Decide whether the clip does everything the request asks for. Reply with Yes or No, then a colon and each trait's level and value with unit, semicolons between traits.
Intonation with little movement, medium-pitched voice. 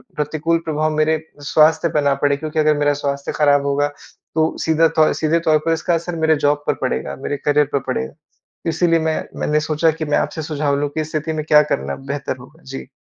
Yes: narrow, 1.8 semitones; medium, 150 Hz